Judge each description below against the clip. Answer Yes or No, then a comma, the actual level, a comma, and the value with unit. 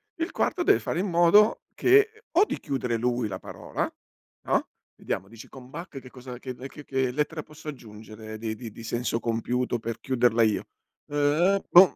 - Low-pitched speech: Yes, low, 130 Hz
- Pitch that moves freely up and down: Yes, wide, 5.9 semitones